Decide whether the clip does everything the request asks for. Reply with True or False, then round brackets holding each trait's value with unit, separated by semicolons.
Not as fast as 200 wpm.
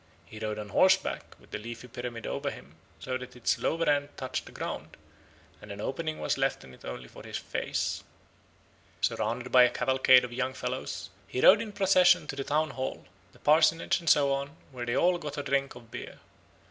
False (205 wpm)